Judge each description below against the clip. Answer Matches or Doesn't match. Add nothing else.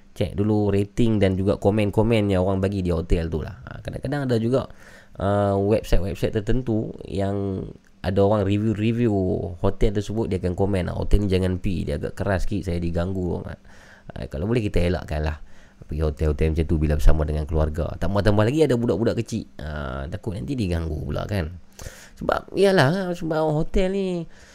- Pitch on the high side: Doesn't match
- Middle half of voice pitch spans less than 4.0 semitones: Doesn't match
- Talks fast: Matches